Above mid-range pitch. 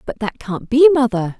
Yes: high, 240 Hz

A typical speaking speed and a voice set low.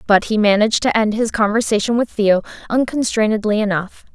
No: average, 160 wpm; high, 215 Hz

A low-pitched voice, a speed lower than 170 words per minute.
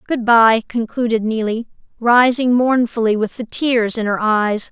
No: high, 230 Hz; average, 155 wpm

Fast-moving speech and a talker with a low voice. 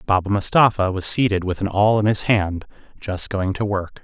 Yes: fast, 210 wpm; low, 100 Hz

